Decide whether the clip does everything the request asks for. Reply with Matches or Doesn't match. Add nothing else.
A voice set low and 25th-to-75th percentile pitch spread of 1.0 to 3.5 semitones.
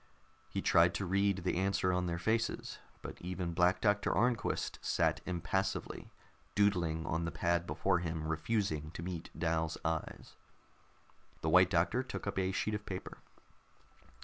Matches